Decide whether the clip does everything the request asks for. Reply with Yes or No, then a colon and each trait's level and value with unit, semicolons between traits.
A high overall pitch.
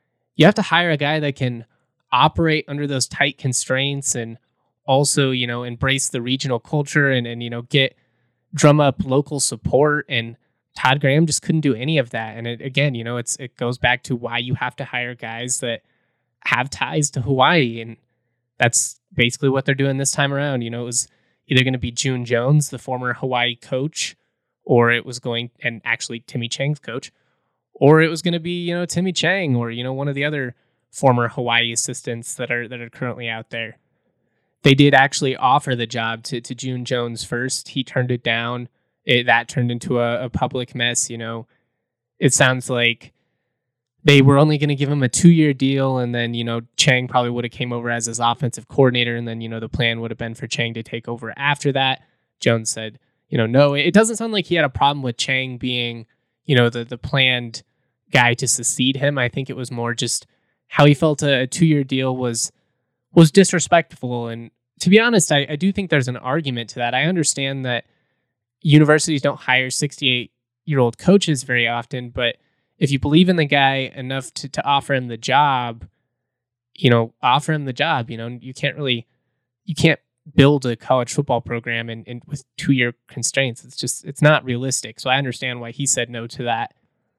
No: low, 130 Hz